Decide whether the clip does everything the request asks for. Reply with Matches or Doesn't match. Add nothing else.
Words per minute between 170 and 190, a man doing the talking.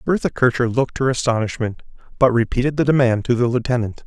Matches